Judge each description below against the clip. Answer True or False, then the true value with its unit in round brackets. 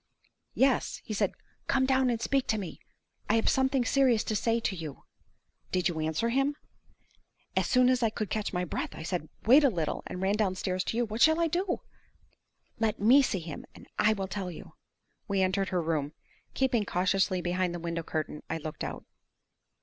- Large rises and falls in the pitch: True (5.7 semitones)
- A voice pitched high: True (205 Hz)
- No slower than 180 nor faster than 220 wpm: True (195 wpm)